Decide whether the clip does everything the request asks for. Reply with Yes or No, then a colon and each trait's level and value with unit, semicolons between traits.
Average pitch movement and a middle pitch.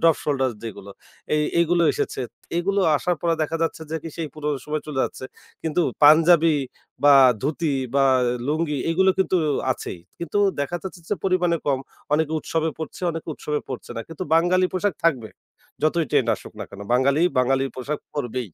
Yes: average, 3.5 semitones; medium, 155 Hz